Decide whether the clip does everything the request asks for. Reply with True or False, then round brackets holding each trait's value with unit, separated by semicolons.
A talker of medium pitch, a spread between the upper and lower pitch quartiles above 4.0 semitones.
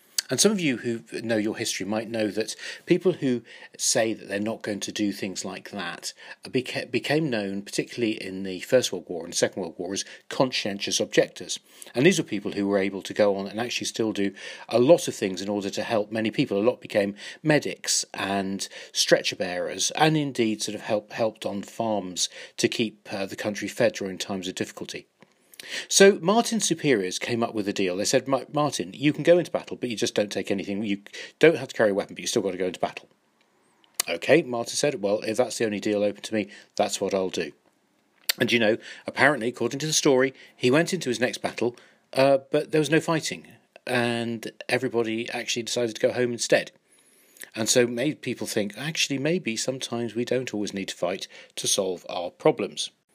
False (115 Hz; 4.6 semitones)